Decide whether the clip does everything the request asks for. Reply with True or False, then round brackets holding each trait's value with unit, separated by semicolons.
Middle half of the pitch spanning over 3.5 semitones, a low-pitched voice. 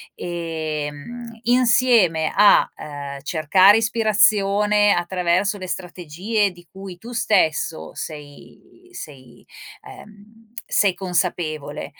False (5.1 semitones; 185 Hz)